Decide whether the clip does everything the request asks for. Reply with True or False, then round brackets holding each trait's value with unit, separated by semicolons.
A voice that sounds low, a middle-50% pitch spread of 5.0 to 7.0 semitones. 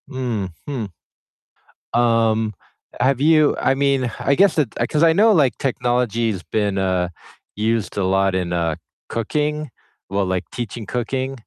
True (120 Hz; 5.4 semitones)